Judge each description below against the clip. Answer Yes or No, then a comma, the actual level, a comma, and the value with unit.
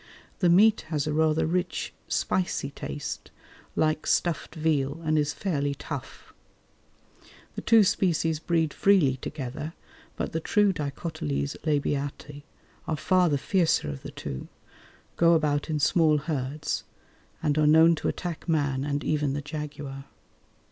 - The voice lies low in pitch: No, medium, 155 Hz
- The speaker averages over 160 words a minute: No, average, 140 wpm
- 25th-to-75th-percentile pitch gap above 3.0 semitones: No, narrow, 2.6 semitones